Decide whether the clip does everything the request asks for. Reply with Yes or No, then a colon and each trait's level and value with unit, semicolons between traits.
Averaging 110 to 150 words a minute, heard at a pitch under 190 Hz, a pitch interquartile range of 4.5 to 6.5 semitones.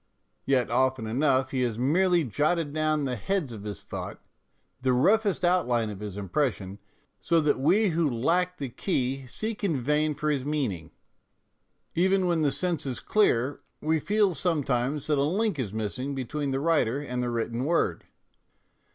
No: average, 170 wpm; medium, 140 Hz; average, 5.1 semitones